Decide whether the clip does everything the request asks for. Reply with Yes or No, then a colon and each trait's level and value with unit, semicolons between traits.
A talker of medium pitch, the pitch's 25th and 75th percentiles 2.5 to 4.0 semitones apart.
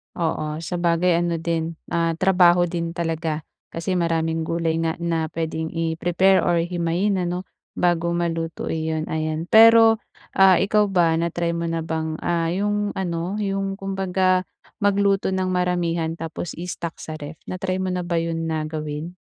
No: medium, 170 Hz; narrow, 2.1 semitones